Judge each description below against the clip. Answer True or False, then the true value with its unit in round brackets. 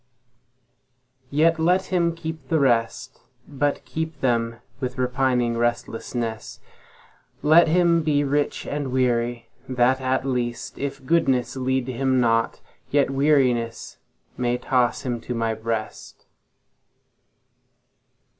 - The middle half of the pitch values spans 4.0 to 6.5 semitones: False (3.3 semitones)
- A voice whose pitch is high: False (130 Hz)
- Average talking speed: False (100 wpm)